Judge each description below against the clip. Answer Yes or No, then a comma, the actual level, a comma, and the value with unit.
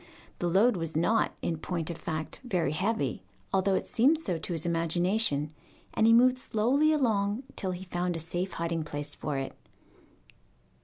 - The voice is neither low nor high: Yes, medium, 180 Hz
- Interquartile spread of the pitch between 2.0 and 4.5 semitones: No, average, 5.3 semitones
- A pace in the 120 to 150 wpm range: No, average, 170 wpm